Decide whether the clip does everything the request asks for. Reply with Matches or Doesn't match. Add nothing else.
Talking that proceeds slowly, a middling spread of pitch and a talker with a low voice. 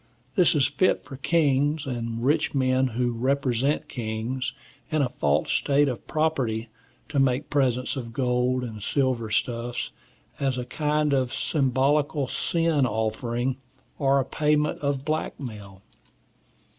Matches